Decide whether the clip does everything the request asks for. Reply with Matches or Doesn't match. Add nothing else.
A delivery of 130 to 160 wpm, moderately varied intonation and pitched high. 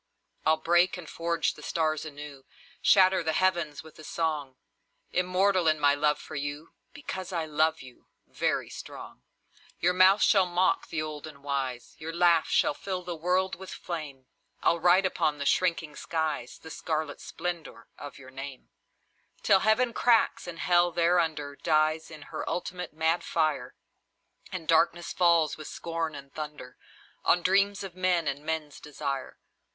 Doesn't match